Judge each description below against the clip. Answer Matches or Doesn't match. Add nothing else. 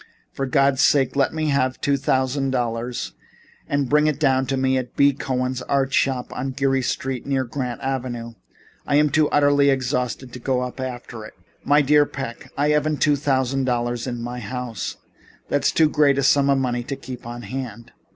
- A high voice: Doesn't match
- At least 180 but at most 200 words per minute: Matches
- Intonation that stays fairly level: Matches